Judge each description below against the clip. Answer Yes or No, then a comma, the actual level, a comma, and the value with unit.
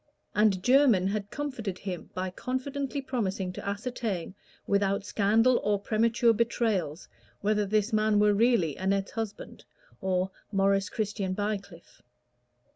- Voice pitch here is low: No, high, 205 Hz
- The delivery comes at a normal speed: No, slow, 120 wpm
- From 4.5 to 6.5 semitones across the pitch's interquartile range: No, average, 3.0 semitones